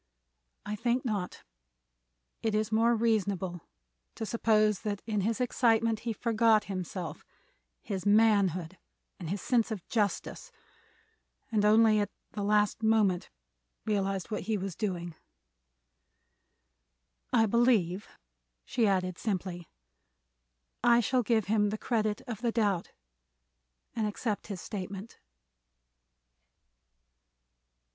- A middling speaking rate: No, slow, 105 wpm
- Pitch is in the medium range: No, high, 210 Hz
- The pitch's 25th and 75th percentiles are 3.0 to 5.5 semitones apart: No, narrow, 2.6 semitones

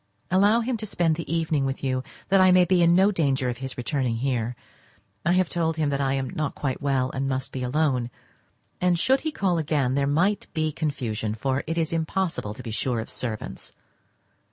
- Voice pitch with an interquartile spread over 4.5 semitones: Yes, average, 4.9 semitones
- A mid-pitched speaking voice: Yes, medium, 145 Hz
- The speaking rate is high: Yes, fast, 210 wpm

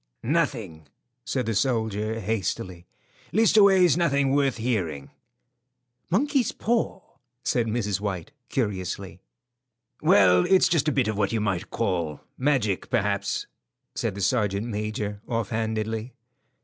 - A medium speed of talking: No, slow, 115 wpm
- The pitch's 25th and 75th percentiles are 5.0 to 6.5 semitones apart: Yes, wide, 5.5 semitones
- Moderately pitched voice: No, low, 110 Hz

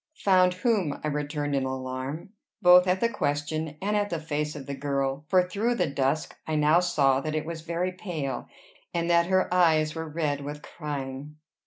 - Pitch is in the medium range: Yes, medium, 155 Hz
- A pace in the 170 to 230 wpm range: Yes, average, 190 wpm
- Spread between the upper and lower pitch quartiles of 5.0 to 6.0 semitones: No, average, 3.8 semitones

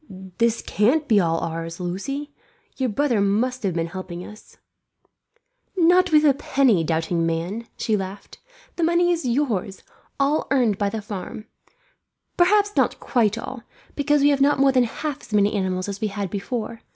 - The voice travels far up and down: Yes, wide, 6.4 semitones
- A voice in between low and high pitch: No, high, 225 Hz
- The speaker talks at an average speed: Yes, average, 170 wpm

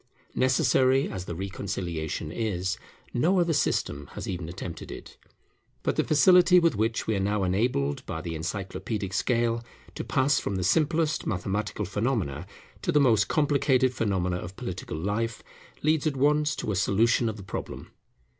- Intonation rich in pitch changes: Yes, wide, 6.4 semitones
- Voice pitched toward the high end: No, low, 105 Hz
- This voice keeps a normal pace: Yes, average, 160 wpm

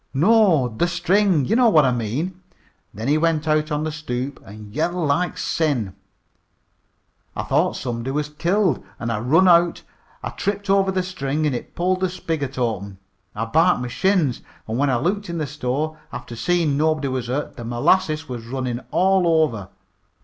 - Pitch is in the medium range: Yes, medium, 150 Hz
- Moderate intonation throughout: No, wide, 6.1 semitones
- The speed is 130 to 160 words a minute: No, average, 180 wpm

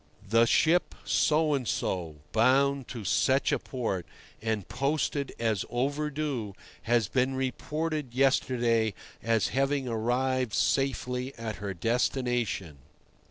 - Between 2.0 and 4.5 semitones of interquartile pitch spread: Yes, average, 3.4 semitones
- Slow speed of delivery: Yes, slow, 115 wpm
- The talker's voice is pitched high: No, low, 125 Hz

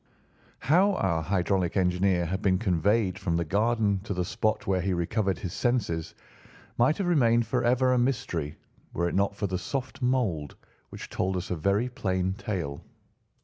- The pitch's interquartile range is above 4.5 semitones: Yes, average, 4.9 semitones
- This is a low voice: Yes, low, 100 Hz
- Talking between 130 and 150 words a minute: No, average, 170 wpm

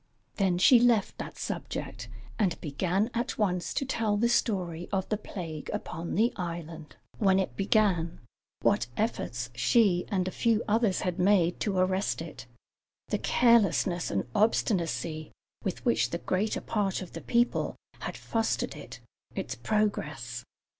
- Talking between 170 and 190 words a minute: No, average, 145 wpm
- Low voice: No, high, 190 Hz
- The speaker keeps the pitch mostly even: No, average, 4.3 semitones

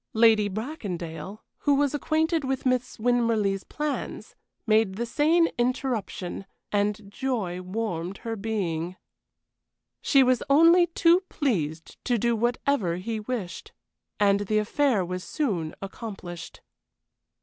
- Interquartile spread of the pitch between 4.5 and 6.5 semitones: Yes, wide, 5.5 semitones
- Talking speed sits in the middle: No, slow, 115 wpm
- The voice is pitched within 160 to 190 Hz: No, high, 220 Hz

